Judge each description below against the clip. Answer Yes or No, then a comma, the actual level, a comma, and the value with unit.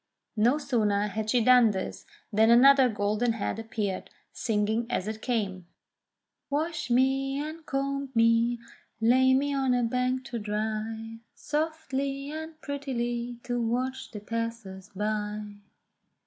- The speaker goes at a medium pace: No, slow, 130 wpm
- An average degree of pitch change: Yes, average, 3.8 semitones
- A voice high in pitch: Yes, high, 235 Hz